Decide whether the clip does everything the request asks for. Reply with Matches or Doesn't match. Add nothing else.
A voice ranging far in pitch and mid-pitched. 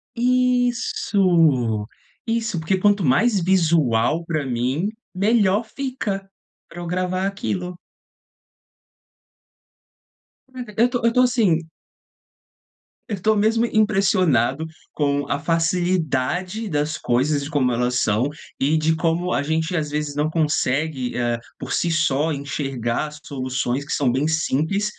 Matches